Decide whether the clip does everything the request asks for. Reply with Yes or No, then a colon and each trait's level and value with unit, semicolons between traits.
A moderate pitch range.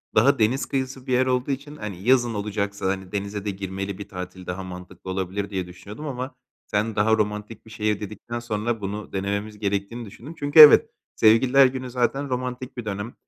Yes: average, 4.1 semitones